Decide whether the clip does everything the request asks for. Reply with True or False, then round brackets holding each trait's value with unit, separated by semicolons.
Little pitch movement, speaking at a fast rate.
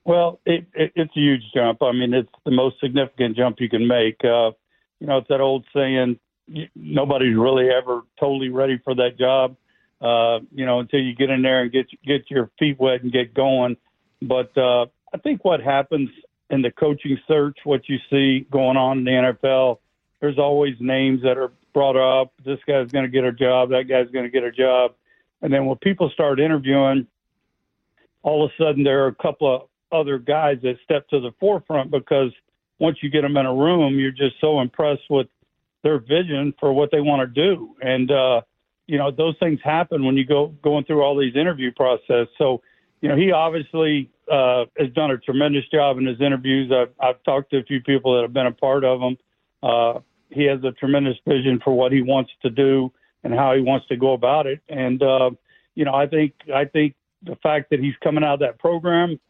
True (2.2 semitones; 215 wpm)